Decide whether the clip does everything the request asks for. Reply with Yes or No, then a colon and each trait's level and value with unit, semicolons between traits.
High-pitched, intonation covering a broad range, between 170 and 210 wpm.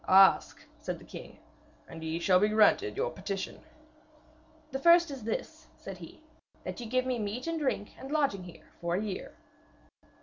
Yes: high, 220 Hz; wide, 7.3 semitones; average, 175 wpm